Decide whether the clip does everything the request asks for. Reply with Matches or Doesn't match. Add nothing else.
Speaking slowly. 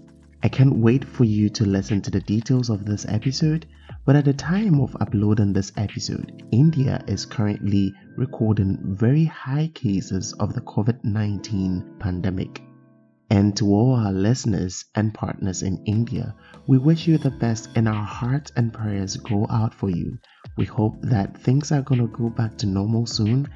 Doesn't match